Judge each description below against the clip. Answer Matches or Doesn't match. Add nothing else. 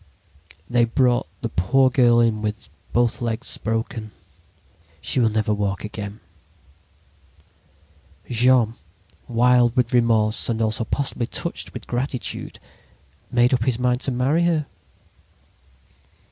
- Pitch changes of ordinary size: Doesn't match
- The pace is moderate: Doesn't match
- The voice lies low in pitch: Matches